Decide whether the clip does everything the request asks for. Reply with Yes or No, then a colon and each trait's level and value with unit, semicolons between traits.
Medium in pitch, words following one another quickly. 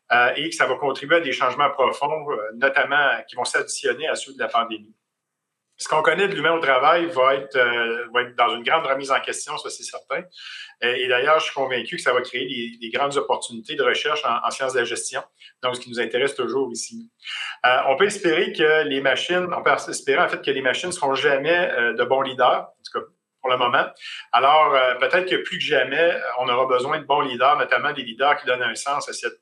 Yes: medium, 155 Hz; fast, 230 wpm